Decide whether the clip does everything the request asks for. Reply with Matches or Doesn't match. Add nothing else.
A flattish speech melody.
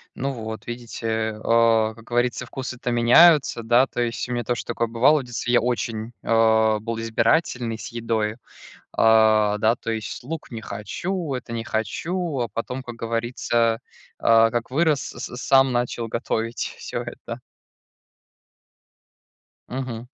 Matches